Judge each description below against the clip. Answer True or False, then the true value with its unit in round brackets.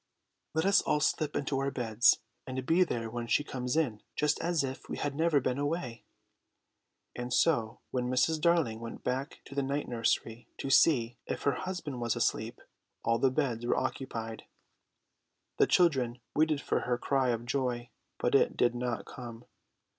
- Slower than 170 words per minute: False (175 wpm)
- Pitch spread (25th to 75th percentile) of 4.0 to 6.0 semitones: False (3.6 semitones)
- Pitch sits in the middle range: False (130 Hz)